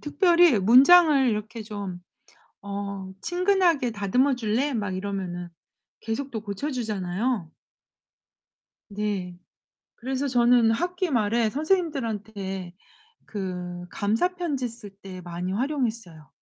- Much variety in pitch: Yes, wide, 5.7 semitones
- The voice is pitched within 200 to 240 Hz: Yes, high, 225 Hz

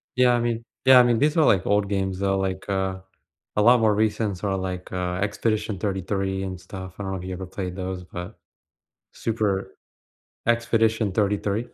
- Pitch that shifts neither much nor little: Yes, average, 3.0 semitones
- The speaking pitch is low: Yes, low, 100 Hz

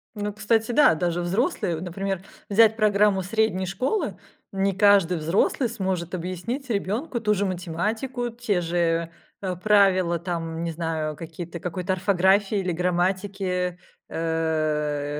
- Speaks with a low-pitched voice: No, medium, 185 Hz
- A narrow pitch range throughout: No, average, 3.5 semitones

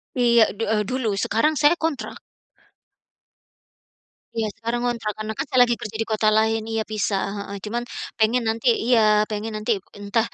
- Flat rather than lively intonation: Yes, narrow, 2.0 semitones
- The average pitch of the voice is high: Yes, high, 225 Hz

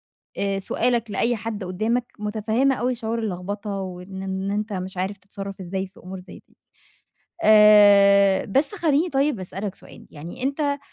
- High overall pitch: Yes, high, 205 Hz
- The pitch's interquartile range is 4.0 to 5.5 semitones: No, average, 3.5 semitones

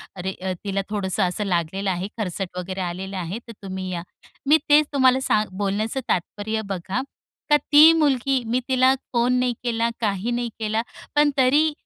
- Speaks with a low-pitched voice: No, high, 215 Hz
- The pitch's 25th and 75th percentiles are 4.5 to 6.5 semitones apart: Yes, average, 5.2 semitones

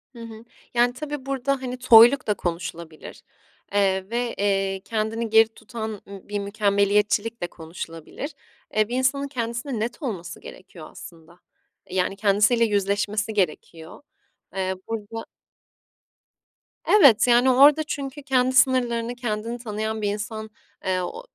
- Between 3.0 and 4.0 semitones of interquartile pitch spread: Yes, average, 3.6 semitones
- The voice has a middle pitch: No, high, 220 Hz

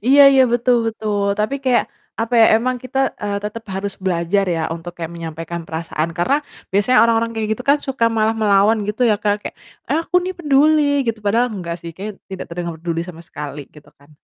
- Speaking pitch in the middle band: No, high, 210 Hz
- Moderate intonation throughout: No, wide, 5.8 semitones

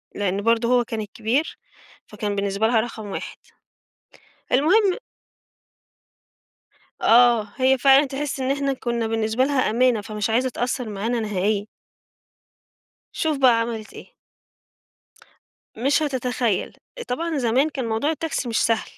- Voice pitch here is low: No, high, 240 Hz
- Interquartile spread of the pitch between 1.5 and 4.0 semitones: Yes, average, 3.4 semitones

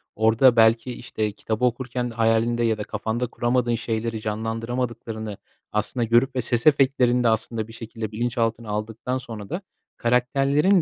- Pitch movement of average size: No, narrow, 1.9 semitones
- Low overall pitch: Yes, low, 115 Hz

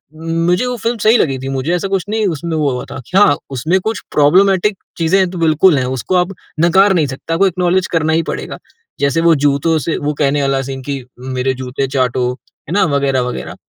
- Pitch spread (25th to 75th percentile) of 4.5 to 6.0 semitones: Yes, average, 5.2 semitones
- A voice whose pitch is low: No, medium, 160 Hz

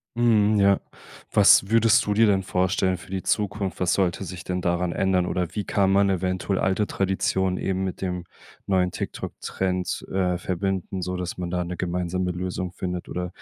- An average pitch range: No, narrow, 1.3 semitones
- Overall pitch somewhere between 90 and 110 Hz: Yes, very low, 95 Hz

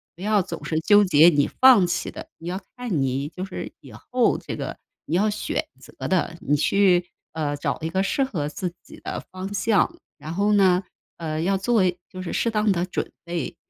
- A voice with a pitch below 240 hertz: Yes, medium, 185 Hz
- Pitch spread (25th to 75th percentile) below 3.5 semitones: No, average, 3.8 semitones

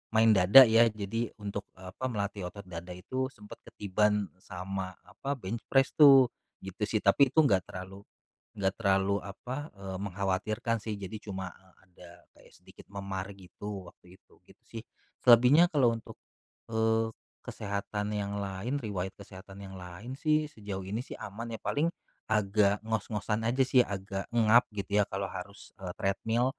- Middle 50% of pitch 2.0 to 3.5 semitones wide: Yes, average, 2.9 semitones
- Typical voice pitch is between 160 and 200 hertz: No, low, 100 Hz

